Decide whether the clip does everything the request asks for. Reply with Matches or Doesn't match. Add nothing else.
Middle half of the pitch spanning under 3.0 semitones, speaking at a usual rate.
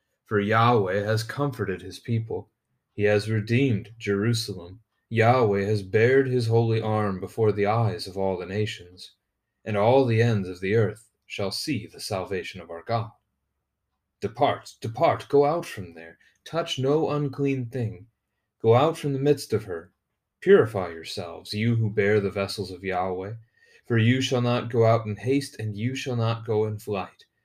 Doesn't match